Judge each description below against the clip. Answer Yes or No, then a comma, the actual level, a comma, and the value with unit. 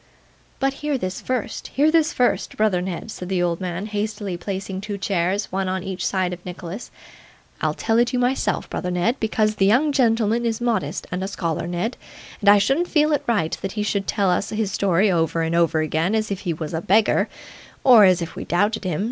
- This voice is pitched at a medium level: No, high, 200 Hz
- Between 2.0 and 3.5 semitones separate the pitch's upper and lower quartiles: No, average, 3.9 semitones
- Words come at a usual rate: No, fast, 220 wpm